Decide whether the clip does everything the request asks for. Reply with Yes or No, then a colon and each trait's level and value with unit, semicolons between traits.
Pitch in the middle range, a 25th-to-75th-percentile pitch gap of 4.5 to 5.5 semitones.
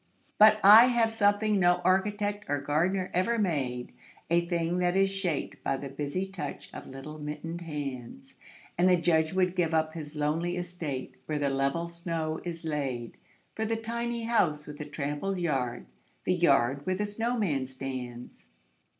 Yes: medium, 170 Hz; average, 4.9 semitones